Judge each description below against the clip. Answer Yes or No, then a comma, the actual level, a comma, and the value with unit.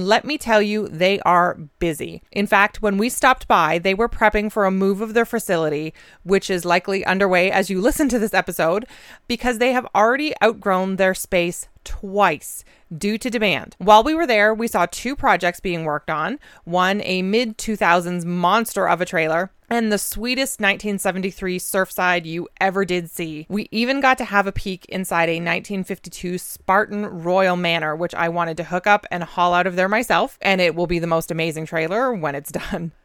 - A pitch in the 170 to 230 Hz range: Yes, high, 190 Hz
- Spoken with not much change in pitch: No, average, 3.5 semitones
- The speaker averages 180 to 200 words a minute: Yes, average, 195 wpm